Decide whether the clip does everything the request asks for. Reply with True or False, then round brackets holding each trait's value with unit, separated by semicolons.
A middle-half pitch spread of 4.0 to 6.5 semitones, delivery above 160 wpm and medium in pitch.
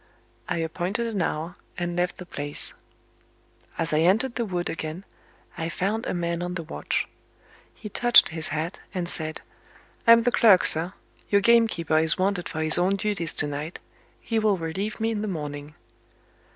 True (4.3 semitones; 175 wpm; 175 Hz)